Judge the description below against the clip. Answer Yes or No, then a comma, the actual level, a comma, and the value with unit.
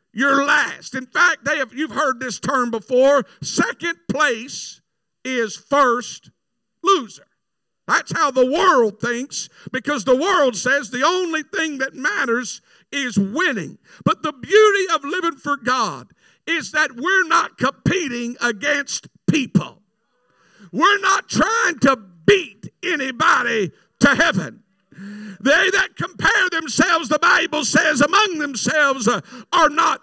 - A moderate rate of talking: No, slow, 130 wpm